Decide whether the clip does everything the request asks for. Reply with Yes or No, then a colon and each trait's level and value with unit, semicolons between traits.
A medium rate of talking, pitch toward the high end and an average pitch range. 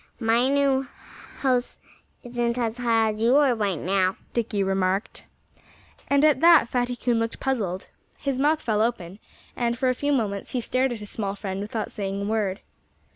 Yes: average, 180 wpm; high, 230 Hz; average, 4.0 semitones